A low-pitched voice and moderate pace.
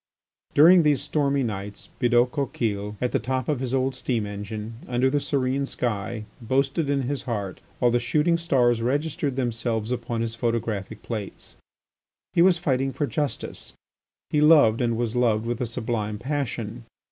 Yes: low, 125 Hz; average, 160 wpm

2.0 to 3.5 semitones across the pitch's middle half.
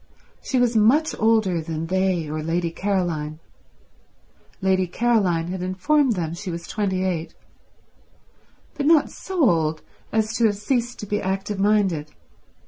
No: average, 4.7 semitones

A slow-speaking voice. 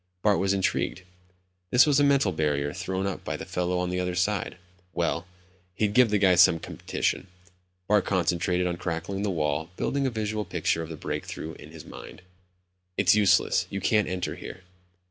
No: average, 185 wpm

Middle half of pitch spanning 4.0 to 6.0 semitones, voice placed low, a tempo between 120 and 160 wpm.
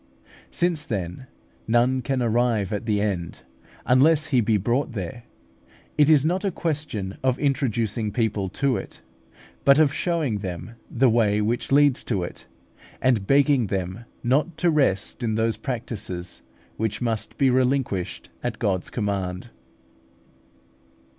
Yes: average, 5.0 semitones; low, 120 Hz; average, 140 wpm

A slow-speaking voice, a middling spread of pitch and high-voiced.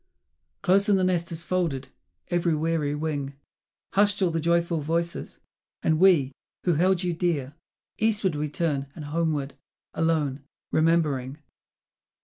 No: slow, 130 wpm; average, 3.0 semitones; medium, 165 Hz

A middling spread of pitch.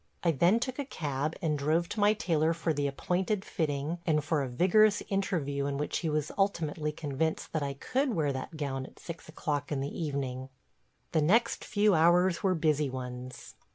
Yes: average, 4.1 semitones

